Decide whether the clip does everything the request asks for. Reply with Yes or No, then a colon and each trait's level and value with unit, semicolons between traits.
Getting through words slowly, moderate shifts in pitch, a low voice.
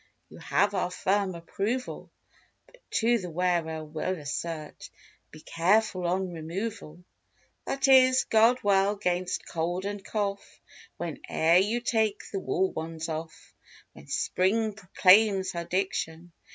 No: slow, 130 wpm; average, 3.9 semitones; medium, 185 Hz